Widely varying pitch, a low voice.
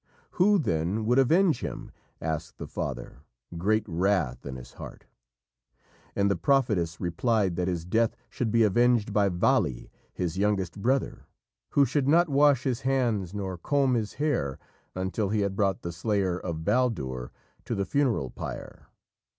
Yes: wide, 6.1 semitones; low, 100 Hz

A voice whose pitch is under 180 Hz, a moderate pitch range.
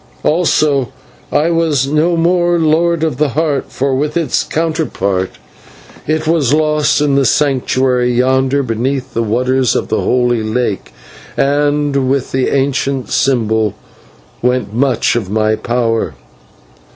Yes: low, 135 Hz; average, 3.7 semitones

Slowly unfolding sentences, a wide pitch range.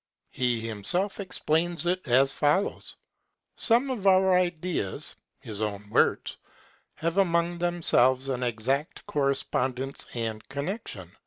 Yes: slow, 110 wpm; wide, 6.5 semitones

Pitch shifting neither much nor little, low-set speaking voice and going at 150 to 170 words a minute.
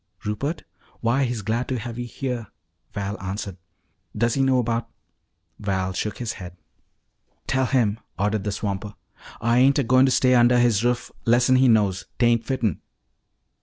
Yes: average, 3.4 semitones; low, 115 Hz; average, 165 wpm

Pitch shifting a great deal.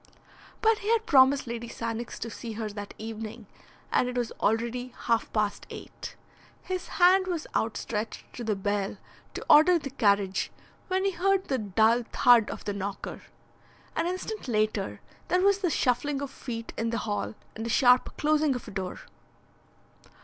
Yes: wide, 6.0 semitones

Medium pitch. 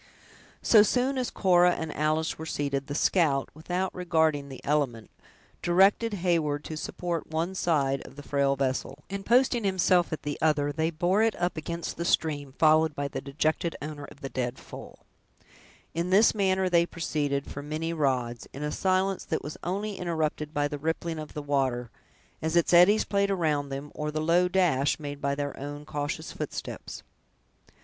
Yes: medium, 155 Hz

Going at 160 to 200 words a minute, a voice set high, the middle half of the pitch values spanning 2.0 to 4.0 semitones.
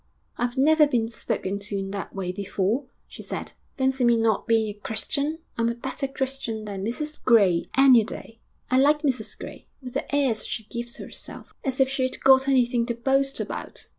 Yes: average, 190 wpm; high, 240 Hz; average, 3.6 semitones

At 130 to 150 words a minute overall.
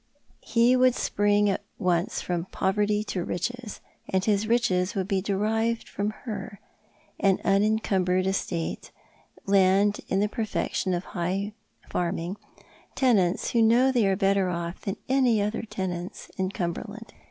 Yes: average, 140 wpm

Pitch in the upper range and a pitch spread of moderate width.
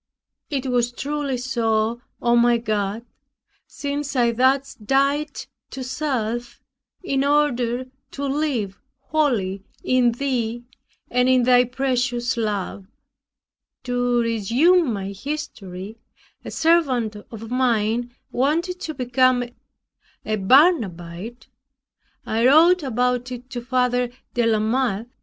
Yes: high, 245 Hz; average, 3.0 semitones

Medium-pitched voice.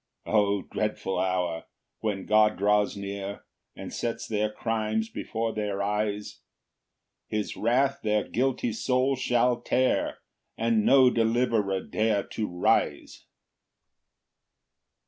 No: low, 110 Hz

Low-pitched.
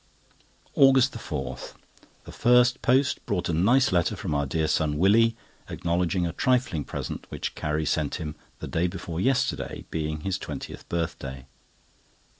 Yes: very low, 85 Hz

